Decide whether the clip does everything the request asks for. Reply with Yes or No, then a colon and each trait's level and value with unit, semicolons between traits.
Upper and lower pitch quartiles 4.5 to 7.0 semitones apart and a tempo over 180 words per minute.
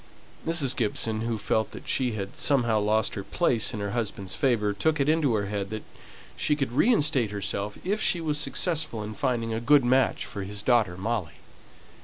Yes: average, 5.1 semitones; average, 190 wpm